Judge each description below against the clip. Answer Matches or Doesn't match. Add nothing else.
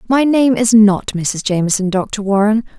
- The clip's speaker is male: Doesn't match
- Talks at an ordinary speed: Matches